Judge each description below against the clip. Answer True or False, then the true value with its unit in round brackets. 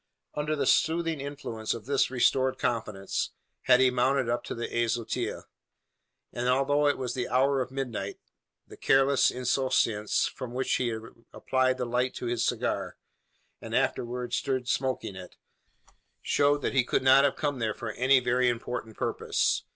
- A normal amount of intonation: False (2.2 semitones)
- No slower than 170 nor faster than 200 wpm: False (160 wpm)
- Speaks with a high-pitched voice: False (125 Hz)